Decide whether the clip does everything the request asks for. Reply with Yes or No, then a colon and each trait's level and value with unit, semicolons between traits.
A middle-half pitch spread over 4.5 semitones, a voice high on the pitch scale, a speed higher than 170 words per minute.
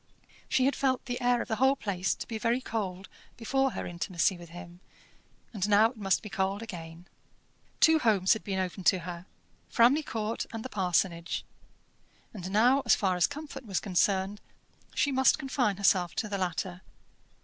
Yes: average, 4.9 semitones; high, 205 Hz; average, 180 wpm